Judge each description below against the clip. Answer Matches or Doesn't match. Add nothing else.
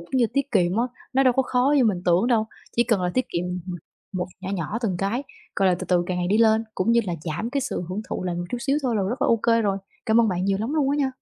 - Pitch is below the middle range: Doesn't match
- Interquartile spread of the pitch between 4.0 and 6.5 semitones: Matches